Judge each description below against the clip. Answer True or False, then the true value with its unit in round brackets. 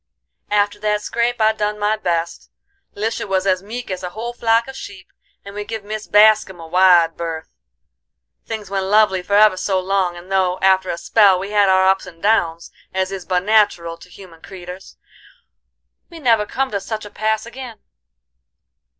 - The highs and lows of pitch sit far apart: False (2.8 semitones)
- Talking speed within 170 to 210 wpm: True (185 wpm)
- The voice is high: True (200 Hz)